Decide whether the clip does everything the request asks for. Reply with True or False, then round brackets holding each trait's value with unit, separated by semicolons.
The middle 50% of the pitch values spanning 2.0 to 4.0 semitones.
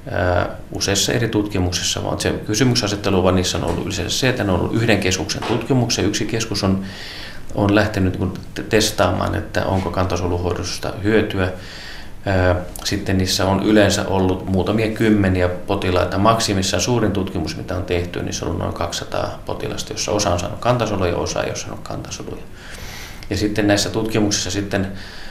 True (2.5 semitones)